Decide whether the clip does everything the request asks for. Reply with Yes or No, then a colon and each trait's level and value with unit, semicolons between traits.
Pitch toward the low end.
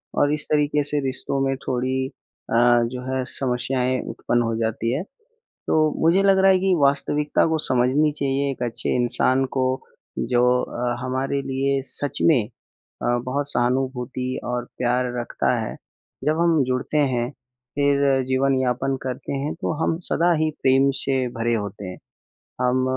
Yes: low, 130 Hz